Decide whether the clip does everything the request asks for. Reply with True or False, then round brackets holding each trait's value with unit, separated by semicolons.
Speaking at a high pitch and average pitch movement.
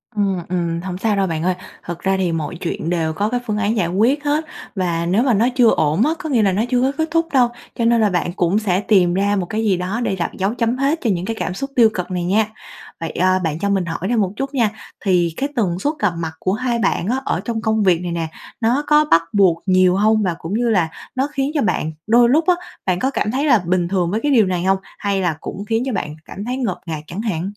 True (200 Hz; 4.9 semitones)